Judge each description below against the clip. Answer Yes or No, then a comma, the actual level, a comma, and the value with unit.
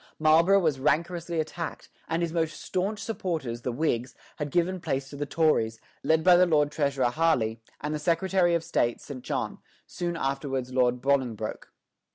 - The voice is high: No, medium, 155 Hz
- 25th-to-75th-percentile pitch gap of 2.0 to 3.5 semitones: No, average, 4.2 semitones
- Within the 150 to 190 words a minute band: Yes, average, 170 wpm